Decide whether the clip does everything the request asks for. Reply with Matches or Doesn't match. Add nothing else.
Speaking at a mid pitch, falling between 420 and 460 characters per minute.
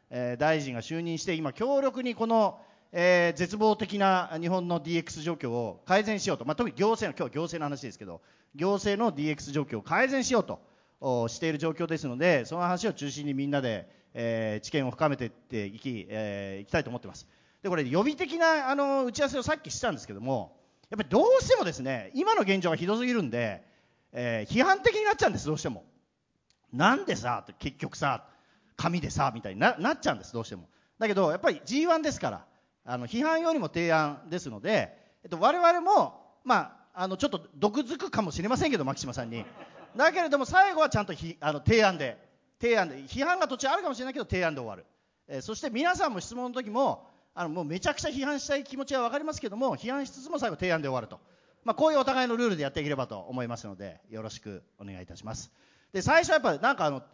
Matches